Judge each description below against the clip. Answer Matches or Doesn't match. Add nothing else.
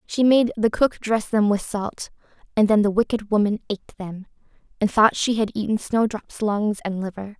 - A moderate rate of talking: Matches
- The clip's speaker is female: Matches